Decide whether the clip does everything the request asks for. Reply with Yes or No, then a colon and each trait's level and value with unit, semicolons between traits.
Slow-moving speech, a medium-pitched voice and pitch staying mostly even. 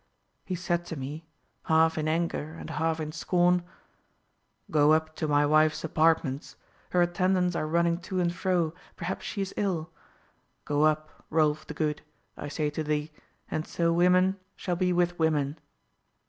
No: average, 160 wpm; medium, 160 Hz; narrow, 2.3 semitones